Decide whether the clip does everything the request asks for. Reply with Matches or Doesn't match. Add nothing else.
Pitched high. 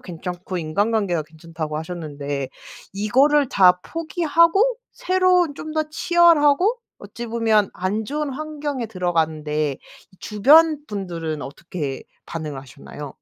Matches